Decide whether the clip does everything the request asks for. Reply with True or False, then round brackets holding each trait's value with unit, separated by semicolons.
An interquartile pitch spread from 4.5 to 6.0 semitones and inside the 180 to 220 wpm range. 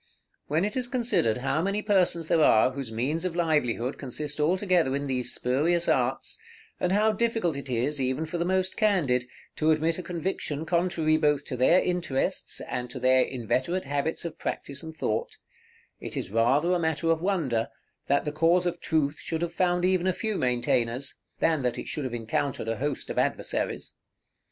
True (5.2 semitones; 185 wpm)